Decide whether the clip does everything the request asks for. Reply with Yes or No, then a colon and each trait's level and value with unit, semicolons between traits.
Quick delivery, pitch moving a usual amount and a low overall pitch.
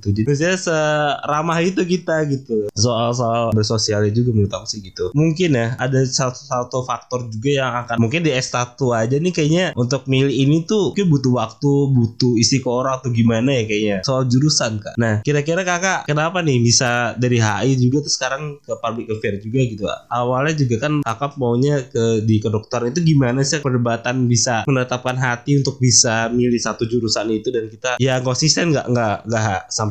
Yes: fast, 180 wpm; average, 3.6 semitones; low, 125 Hz